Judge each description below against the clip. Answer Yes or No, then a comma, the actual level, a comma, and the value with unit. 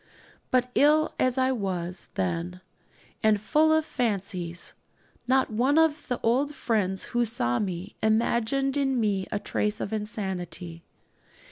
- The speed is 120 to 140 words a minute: Yes, slow, 135 wpm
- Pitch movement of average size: No, wide, 5.7 semitones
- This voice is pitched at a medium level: No, high, 220 Hz